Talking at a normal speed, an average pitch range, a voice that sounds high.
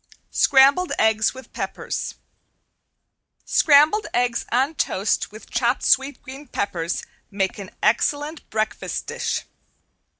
No: slow, 105 wpm; average, 5.0 semitones; high, 245 Hz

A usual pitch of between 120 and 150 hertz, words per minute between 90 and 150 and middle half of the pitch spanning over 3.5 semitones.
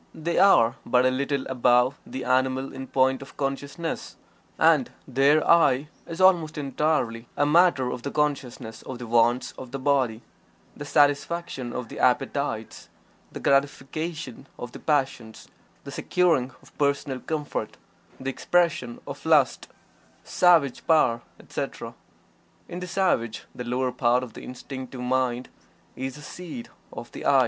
No: low, 135 Hz; average, 145 wpm; average, 3.2 semitones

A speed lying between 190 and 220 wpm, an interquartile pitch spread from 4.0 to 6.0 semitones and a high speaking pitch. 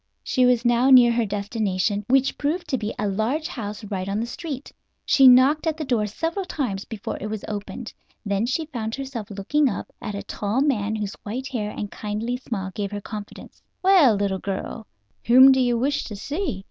Yes: average, 200 wpm; average, 4.4 semitones; high, 230 Hz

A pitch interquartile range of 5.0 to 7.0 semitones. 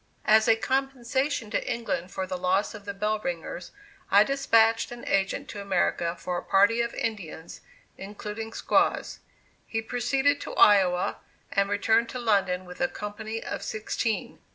No: average, 3.2 semitones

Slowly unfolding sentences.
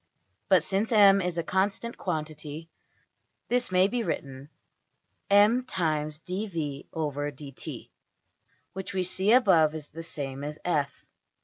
Yes: slow, 110 wpm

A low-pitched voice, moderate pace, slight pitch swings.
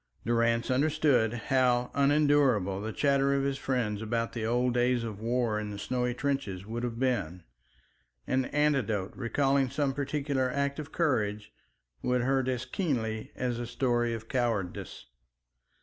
No: low, 125 Hz; average, 150 wpm; average, 3.4 semitones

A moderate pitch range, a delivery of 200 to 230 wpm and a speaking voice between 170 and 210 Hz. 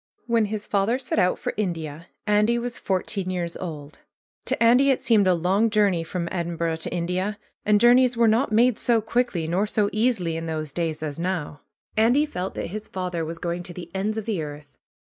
Yes: average, 4.7 semitones; fast, 205 wpm; high, 190 Hz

